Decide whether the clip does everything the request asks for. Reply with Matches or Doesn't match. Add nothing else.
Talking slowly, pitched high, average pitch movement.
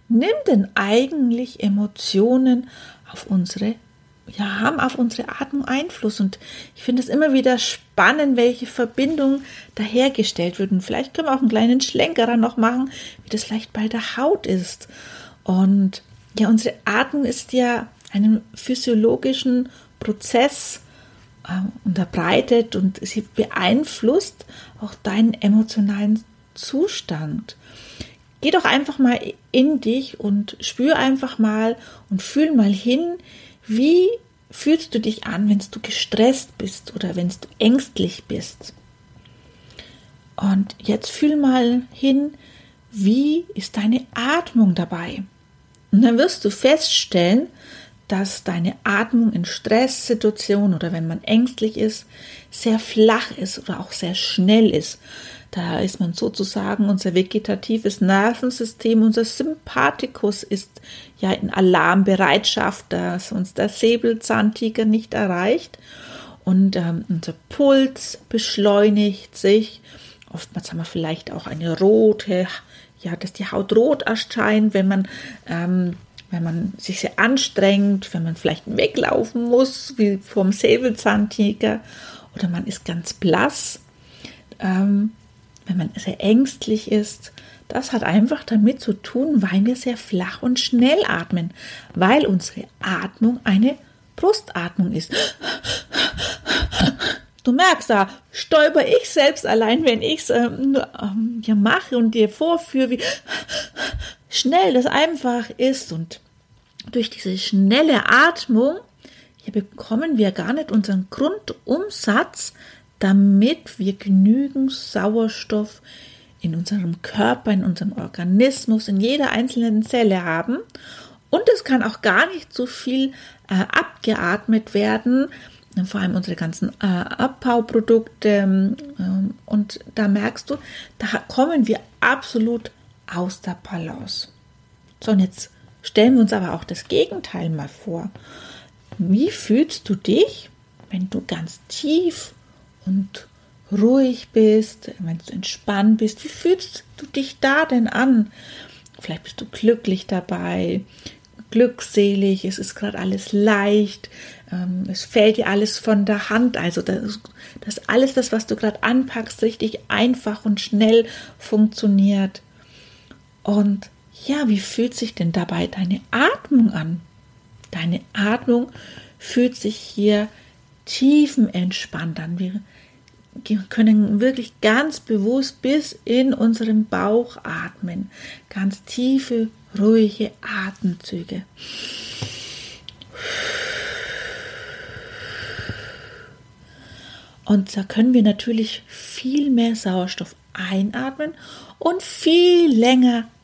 Matches